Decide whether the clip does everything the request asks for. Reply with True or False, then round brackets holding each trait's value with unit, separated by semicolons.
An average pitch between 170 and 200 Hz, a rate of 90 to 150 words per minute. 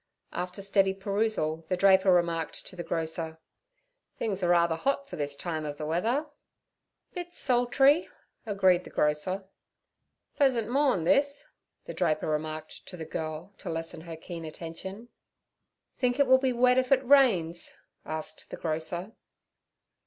True (185 Hz; 145 wpm)